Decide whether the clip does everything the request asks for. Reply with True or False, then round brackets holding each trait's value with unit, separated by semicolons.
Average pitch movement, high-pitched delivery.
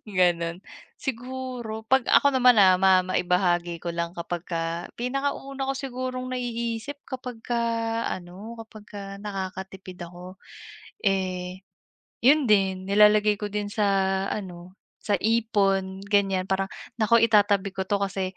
True (4.0 semitones; 200 Hz)